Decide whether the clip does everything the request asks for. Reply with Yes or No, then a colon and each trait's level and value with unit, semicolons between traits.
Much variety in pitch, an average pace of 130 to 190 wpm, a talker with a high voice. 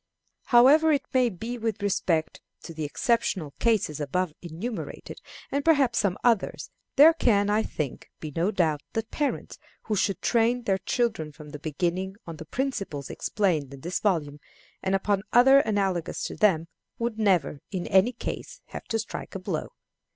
Yes: wide, 6.2 semitones; average, 165 wpm; high, 200 Hz